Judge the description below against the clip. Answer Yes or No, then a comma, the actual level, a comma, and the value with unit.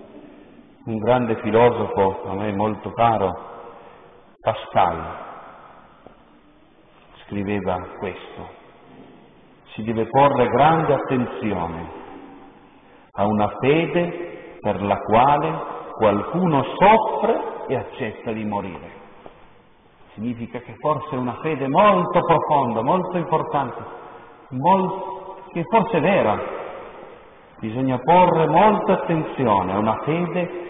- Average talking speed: No, slow, 95 wpm